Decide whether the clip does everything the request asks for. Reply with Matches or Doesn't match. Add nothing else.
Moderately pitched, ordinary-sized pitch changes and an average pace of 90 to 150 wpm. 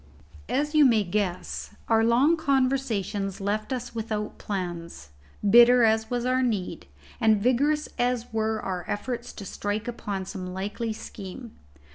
Doesn't match